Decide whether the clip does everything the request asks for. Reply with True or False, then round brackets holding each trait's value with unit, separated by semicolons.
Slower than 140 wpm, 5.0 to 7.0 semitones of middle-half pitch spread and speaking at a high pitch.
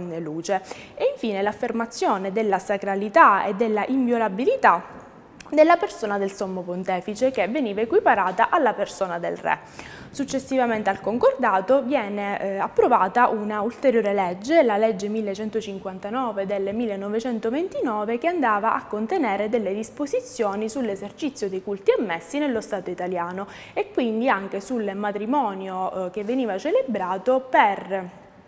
False (120 wpm; 4.4 semitones; 215 Hz)